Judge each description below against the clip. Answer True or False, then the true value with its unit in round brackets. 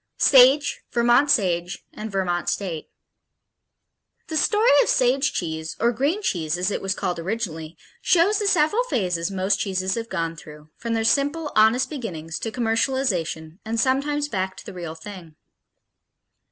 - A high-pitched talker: True (215 Hz)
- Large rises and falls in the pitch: True (7.4 semitones)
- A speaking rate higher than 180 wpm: False (155 wpm)